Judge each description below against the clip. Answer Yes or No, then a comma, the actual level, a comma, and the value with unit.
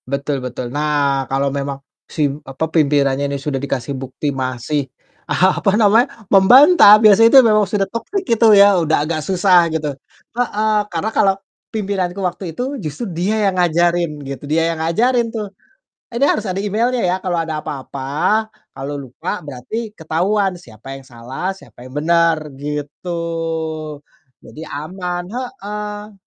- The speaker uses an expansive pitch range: Yes, wide, 6.5 semitones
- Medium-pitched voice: Yes, medium, 170 Hz